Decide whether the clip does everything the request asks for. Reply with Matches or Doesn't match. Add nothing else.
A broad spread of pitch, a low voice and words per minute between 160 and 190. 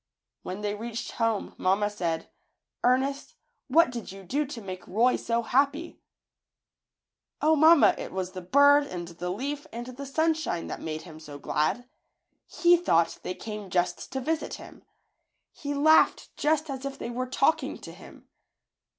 Doesn't match